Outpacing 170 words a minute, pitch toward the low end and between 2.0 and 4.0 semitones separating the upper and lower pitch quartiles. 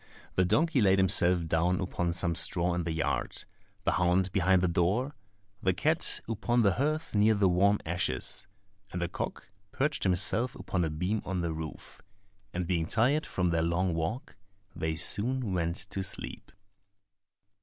No: average, 165 wpm; very low, 90 Hz; average, 3.5 semitones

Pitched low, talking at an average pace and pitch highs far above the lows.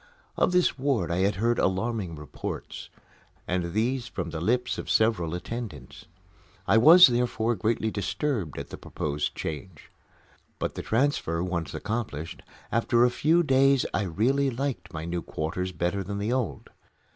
Yes: low, 110 Hz; average, 155 wpm; wide, 6.0 semitones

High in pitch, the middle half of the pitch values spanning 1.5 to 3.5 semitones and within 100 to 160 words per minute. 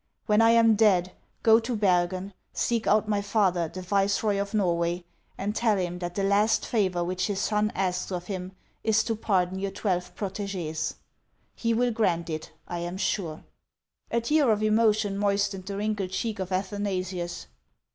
No: high, 200 Hz; average, 2.9 semitones; average, 170 wpm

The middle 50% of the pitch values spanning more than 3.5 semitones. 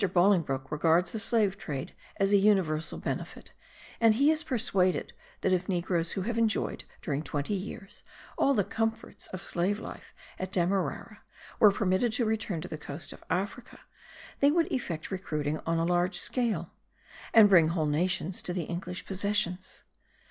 Yes: average, 4.1 semitones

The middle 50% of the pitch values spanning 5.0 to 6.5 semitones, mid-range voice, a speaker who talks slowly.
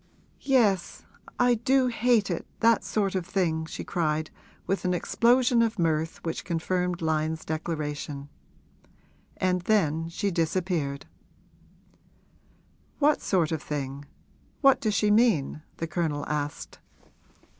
Yes: average, 5.3 semitones; medium, 175 Hz; slow, 120 wpm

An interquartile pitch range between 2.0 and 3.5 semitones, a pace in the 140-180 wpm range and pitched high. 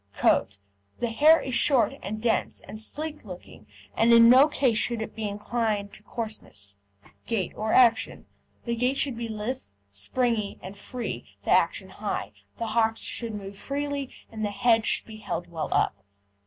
Yes: average, 2.9 semitones; average, 170 wpm; high, 225 Hz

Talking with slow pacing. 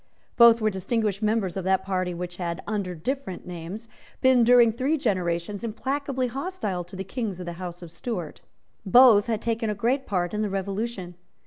No: average, 185 wpm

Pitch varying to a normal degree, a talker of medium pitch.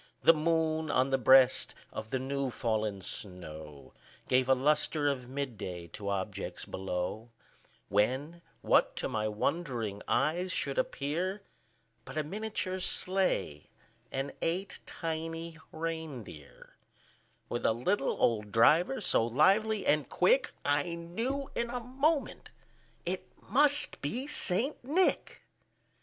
No: wide, 7.8 semitones; medium, 145 Hz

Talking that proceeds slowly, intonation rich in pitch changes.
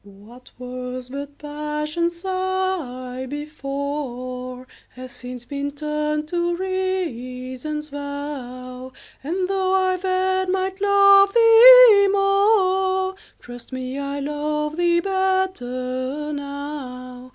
Yes: slow, 95 wpm; wide, 6.6 semitones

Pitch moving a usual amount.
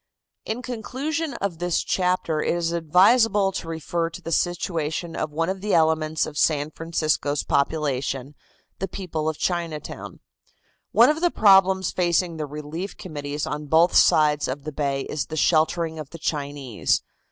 Yes: average, 3.3 semitones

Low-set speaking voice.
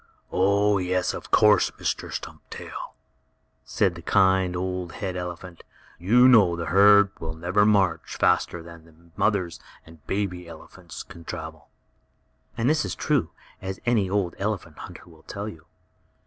Yes: very low, 95 Hz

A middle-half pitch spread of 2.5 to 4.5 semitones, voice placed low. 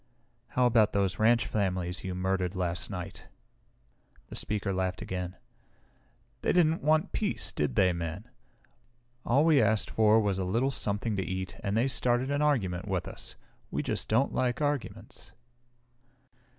No: average, 5.1 semitones; low, 105 Hz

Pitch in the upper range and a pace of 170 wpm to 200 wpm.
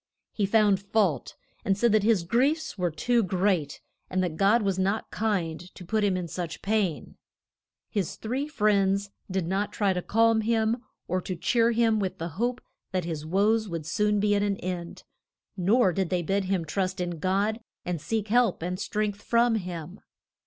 Yes: high, 200 Hz; average, 185 wpm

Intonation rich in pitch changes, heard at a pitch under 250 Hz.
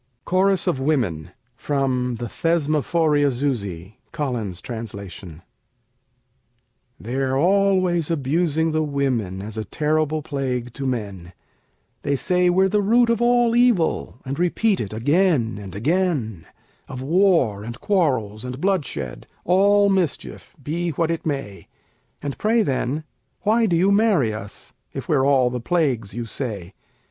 Yes: wide, 7.2 semitones; medium, 140 Hz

